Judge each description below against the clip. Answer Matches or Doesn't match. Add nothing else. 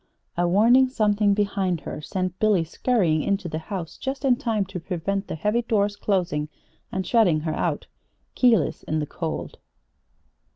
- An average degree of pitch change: Matches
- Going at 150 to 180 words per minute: Matches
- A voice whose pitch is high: Matches